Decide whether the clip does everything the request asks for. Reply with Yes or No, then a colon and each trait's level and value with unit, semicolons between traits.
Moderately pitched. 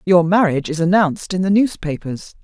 Yes: medium, 180 Hz